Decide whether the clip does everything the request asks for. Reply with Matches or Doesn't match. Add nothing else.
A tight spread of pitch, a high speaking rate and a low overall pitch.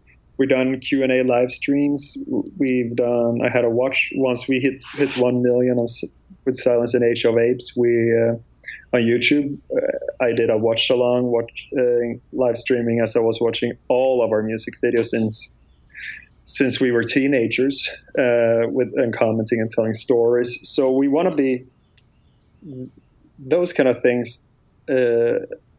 Doesn't match